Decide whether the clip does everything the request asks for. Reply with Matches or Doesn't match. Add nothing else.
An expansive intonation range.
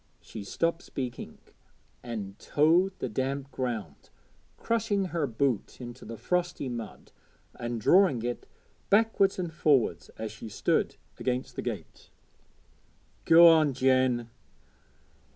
Matches